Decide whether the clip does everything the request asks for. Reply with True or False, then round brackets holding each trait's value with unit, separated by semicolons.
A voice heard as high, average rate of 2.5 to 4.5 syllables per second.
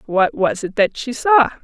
True (235 Hz; 4.3 syllables/s)